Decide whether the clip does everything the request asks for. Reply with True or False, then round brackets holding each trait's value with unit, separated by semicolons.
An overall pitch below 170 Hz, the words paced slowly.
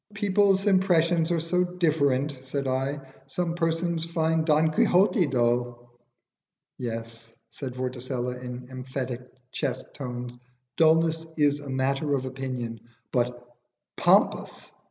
True (140 Hz; 115 wpm)